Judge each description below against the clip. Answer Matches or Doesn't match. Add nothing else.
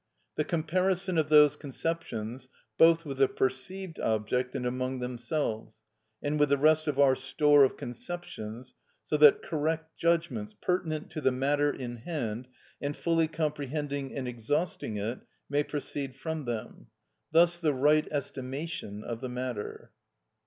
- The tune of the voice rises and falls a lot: Doesn't match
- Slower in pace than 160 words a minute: Matches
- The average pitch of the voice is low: Doesn't match